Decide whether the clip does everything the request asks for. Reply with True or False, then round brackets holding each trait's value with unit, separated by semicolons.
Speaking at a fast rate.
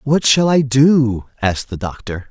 False (180 wpm)